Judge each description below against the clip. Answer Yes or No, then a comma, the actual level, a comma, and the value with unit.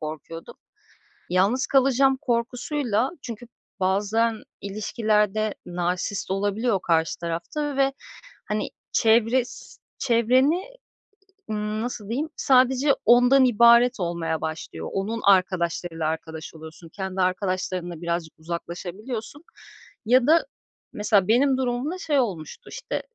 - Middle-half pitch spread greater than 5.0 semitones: Yes, wide, 5.6 semitones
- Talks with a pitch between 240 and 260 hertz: No, high, 215 Hz